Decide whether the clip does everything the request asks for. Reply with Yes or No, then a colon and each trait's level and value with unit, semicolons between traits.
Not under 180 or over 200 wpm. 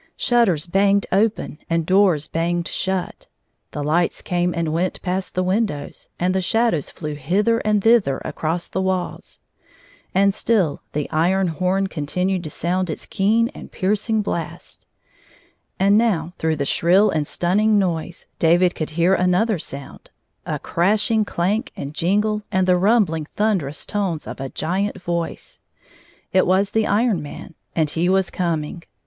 No: average, 155 wpm